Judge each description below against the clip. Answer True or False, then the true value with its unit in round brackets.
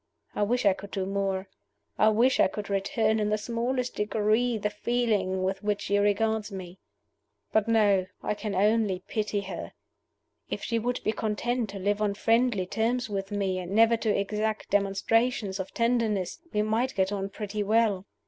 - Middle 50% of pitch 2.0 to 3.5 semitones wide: True (2.4 semitones)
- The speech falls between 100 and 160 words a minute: False (175 wpm)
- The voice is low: False (210 Hz)